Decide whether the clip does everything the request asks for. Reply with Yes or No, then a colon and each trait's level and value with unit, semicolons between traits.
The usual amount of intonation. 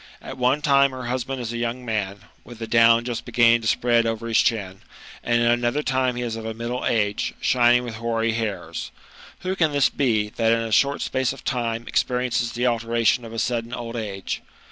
No: narrow, 1.6 semitones